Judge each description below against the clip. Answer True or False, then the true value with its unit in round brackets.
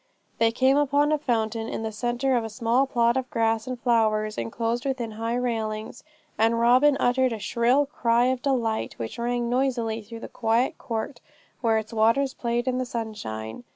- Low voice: False (235 Hz)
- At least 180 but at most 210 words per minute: True (185 wpm)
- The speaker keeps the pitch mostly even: True (2.3 semitones)